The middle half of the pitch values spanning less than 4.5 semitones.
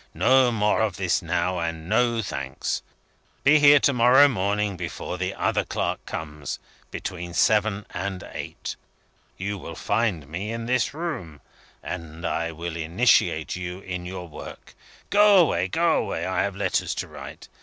No: average, 5.3 semitones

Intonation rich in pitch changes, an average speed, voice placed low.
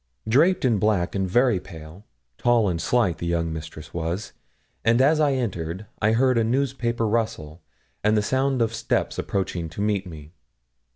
Yes: wide, 5.9 semitones; average, 170 wpm; low, 105 Hz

